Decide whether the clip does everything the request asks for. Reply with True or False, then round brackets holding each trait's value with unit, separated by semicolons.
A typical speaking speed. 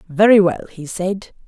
True (160 wpm)